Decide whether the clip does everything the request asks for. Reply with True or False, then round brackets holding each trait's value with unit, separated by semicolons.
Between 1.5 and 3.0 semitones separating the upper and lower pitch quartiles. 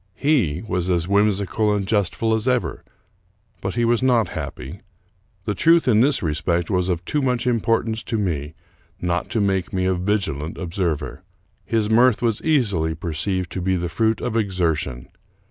False (4.6 semitones)